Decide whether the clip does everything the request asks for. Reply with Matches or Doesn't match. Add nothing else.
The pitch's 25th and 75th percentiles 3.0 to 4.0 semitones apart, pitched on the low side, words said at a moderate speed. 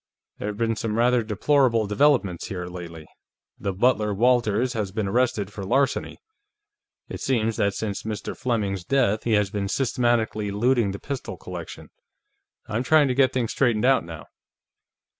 Matches